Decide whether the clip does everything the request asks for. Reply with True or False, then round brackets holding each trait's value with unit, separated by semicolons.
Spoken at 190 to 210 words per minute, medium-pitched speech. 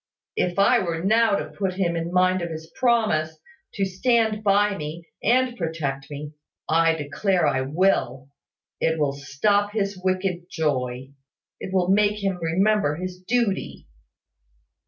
False (145 wpm; 180 Hz)